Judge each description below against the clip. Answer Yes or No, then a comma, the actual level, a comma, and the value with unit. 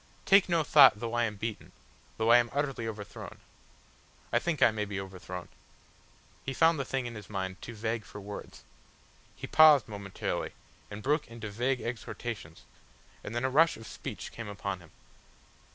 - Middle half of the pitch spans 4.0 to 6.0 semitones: Yes, average, 4.6 semitones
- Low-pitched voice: Yes, low, 115 Hz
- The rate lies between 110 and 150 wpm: No, average, 175 wpm